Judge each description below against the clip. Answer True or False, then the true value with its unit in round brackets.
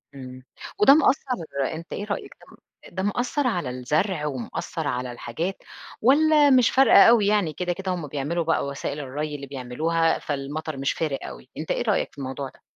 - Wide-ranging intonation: True (6.7 semitones)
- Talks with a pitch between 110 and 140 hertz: False (160 Hz)